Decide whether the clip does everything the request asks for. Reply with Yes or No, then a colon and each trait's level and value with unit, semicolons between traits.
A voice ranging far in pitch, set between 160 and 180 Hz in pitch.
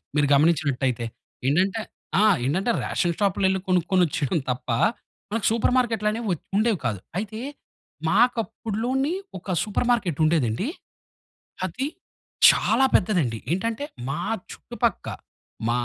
No: wide, 6.7 semitones; high, 190 Hz